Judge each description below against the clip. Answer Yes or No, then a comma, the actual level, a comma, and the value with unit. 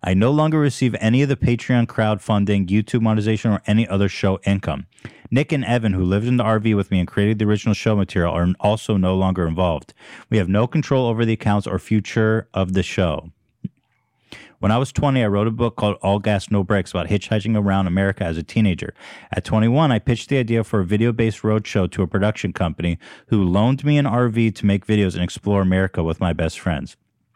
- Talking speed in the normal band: No, fast, 215 wpm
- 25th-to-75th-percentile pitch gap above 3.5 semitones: No, average, 3.1 semitones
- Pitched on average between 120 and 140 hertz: No, low, 105 Hz